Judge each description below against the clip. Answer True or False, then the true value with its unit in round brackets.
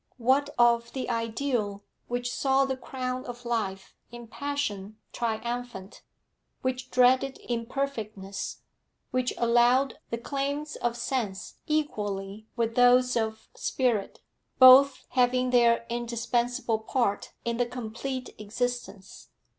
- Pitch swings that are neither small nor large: False (2.3 semitones)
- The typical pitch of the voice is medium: False (240 Hz)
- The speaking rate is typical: False (110 wpm)